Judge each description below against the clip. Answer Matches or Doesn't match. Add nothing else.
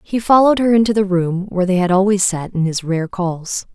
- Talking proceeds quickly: Matches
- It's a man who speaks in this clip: Doesn't match